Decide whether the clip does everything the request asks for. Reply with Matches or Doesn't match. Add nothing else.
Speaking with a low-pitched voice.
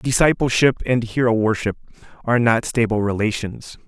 Matches